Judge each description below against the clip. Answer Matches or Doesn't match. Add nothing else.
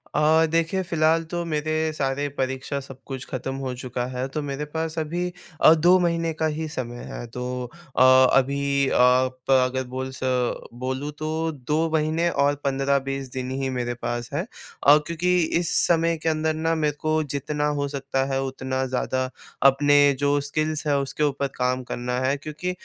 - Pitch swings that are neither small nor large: Matches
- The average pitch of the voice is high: Doesn't match